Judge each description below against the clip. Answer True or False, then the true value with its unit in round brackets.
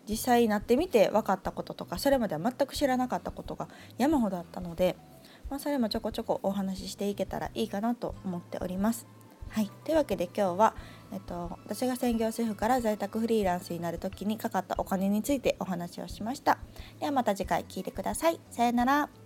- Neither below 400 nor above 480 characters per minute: True (445 characters per minute)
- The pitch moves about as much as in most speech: True (4.4 semitones)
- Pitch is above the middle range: True (215 Hz)